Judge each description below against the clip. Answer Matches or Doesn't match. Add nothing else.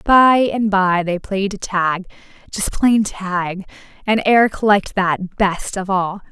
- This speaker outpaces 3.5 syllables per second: Doesn't match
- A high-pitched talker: Matches